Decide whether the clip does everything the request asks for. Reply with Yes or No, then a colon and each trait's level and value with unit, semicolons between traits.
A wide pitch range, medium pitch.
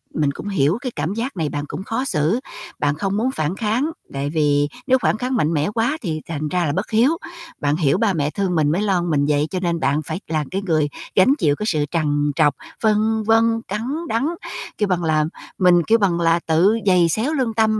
Yes: wide, 6.3 semitones; medium, 180 Hz